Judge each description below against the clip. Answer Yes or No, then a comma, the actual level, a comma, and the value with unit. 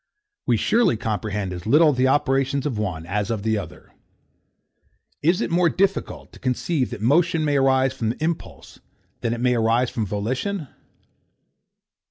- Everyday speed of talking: Yes, average, 160 wpm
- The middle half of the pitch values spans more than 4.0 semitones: Yes, wide, 5.5 semitones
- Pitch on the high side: No, low, 130 Hz